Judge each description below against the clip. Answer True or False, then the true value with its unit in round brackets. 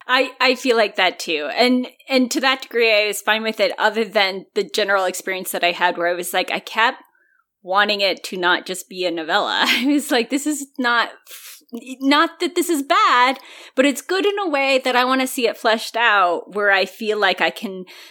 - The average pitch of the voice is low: False (225 Hz)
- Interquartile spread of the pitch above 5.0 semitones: True (5.5 semitones)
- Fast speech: True (230 wpm)